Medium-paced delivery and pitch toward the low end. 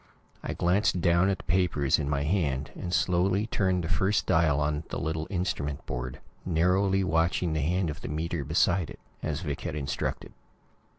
Yes: average, 180 wpm; very low, 85 Hz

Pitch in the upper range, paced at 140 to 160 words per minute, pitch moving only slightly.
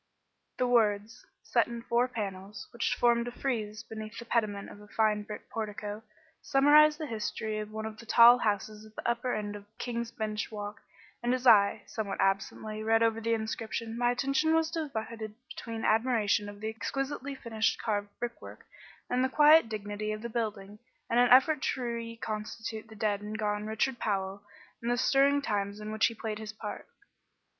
No: high, 220 Hz; average, 185 wpm; narrow, 2.3 semitones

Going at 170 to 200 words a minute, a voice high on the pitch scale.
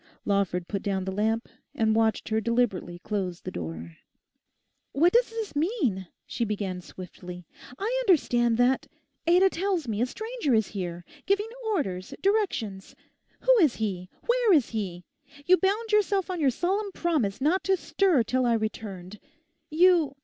No: average, 150 wpm; high, 240 Hz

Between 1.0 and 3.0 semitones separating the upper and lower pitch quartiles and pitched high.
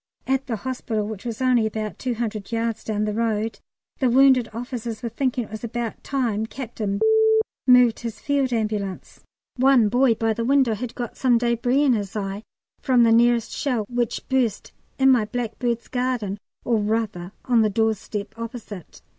Yes: narrow, 2.4 semitones; high, 230 Hz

